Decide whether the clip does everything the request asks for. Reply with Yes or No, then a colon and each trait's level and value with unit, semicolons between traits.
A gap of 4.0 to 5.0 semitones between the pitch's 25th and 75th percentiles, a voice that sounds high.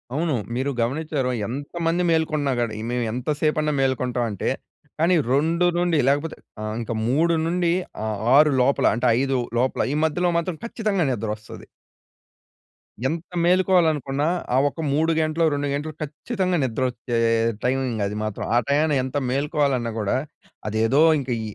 No: average, 4.6 semitones; medium, 145 Hz